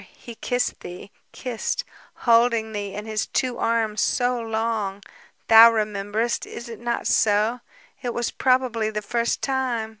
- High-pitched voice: Yes, high, 230 Hz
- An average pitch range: No, narrow, 2.0 semitones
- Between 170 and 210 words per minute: No, average, 145 wpm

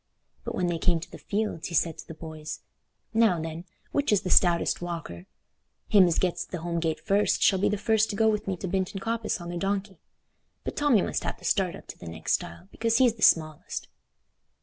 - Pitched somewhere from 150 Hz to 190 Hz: Yes, medium, 185 Hz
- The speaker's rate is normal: No, fast, 230 wpm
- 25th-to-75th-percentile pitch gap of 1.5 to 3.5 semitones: No, average, 4.1 semitones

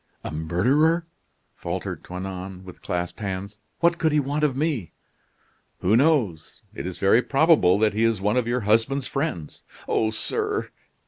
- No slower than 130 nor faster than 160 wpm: Yes, average, 155 wpm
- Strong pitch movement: Yes, wide, 7.7 semitones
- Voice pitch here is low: Yes, low, 110 Hz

